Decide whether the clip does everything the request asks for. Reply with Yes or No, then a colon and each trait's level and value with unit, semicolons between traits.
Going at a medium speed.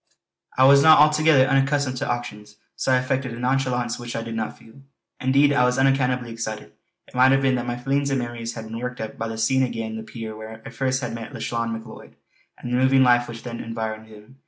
No: fast, 235 wpm